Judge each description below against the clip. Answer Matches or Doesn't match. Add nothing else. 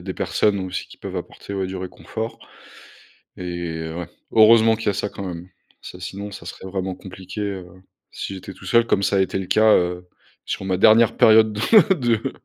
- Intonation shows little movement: Doesn't match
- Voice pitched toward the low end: Matches